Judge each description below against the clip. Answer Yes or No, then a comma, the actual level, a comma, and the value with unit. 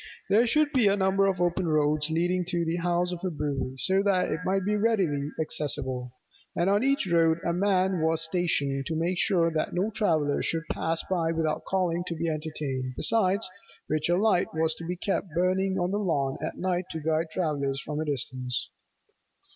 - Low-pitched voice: No, medium, 170 Hz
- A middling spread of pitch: Yes, average, 3.5 semitones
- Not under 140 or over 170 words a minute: No, average, 195 wpm